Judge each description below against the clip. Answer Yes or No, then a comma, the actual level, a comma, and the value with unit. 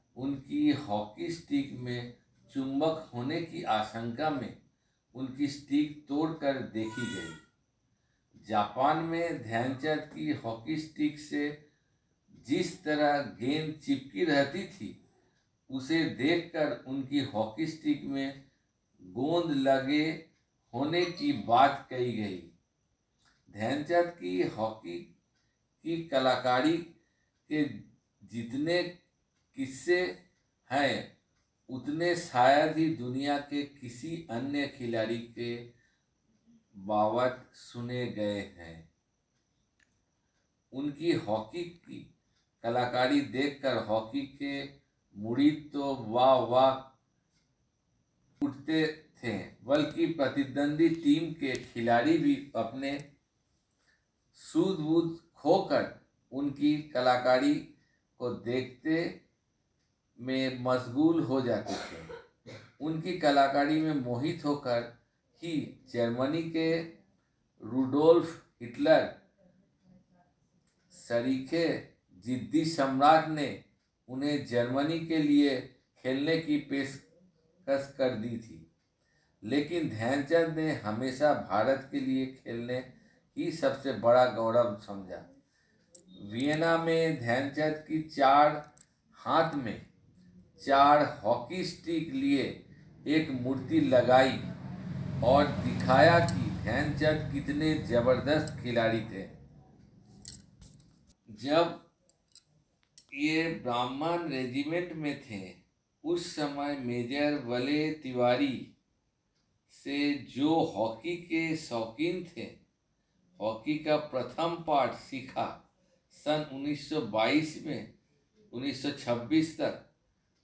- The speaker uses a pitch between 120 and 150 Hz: Yes, medium, 140 Hz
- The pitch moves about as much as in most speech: Yes, average, 4.3 semitones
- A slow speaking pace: Yes, slow, 90 wpm